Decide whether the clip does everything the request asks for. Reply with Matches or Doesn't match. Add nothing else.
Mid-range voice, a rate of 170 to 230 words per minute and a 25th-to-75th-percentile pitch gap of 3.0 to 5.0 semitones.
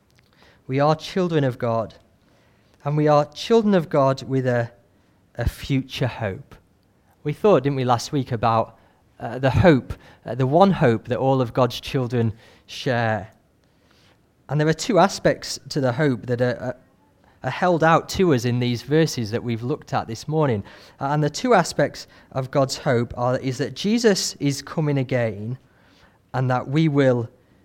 Doesn't match